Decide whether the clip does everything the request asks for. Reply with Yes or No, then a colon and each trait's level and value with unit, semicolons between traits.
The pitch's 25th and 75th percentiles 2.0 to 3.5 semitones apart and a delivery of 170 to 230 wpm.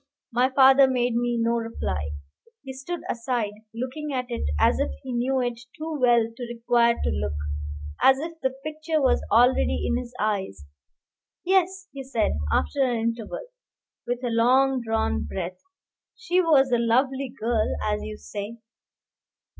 No: average, 2.8 semitones; average, 155 wpm